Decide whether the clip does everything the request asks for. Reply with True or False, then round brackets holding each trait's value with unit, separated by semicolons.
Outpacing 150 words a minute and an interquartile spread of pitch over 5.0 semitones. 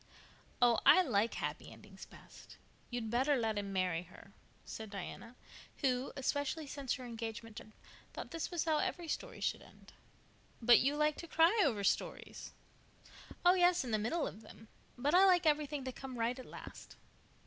True (180 wpm; 5.4 semitones)